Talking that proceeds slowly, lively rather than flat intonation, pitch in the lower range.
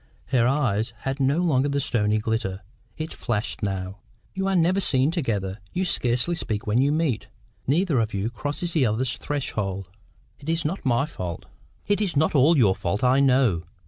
No: average, 180 wpm; wide, 6.7 semitones; low, 130 Hz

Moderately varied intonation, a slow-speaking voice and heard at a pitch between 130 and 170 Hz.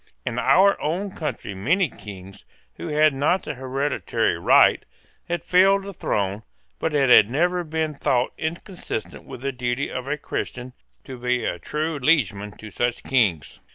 No: average, 5.0 semitones; average, 160 wpm; low, 135 Hz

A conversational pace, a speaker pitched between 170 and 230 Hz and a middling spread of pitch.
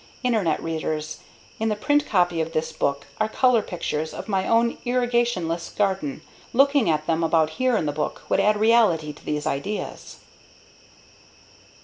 No: average, 160 wpm; medium, 185 Hz; wide, 6.5 semitones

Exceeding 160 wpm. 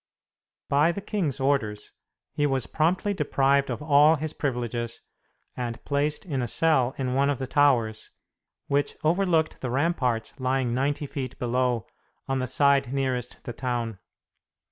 No: average, 145 wpm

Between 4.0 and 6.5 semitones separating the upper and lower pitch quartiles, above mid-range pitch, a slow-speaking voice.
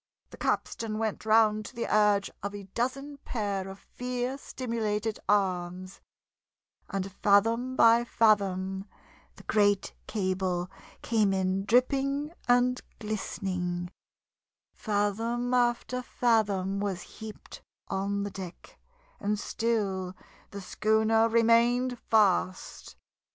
No: average, 3.2 semitones; high, 210 Hz; slow, 105 wpm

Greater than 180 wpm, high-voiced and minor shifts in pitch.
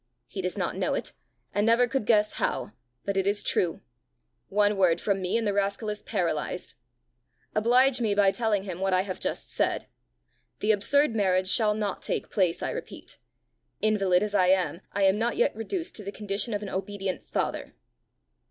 Yes: average, 190 wpm; high, 205 Hz; narrow, 2.2 semitones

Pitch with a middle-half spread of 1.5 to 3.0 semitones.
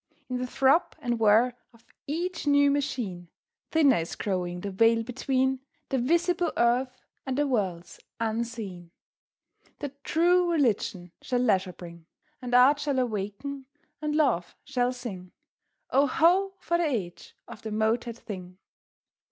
No: wide, 5.6 semitones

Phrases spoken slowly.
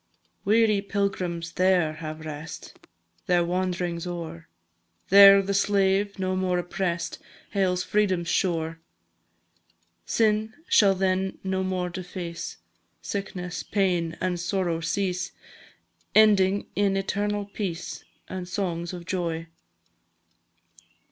Yes: slow, 100 wpm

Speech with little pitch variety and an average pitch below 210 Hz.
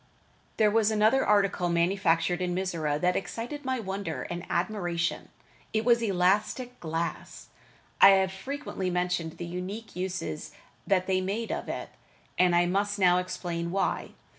No: average, 3.0 semitones; medium, 185 Hz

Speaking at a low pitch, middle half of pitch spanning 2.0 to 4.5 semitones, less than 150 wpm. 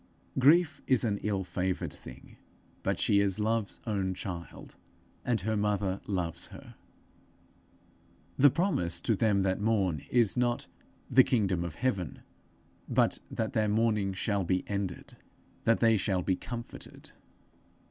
Yes: low, 105 Hz; average, 3.4 semitones; slow, 135 wpm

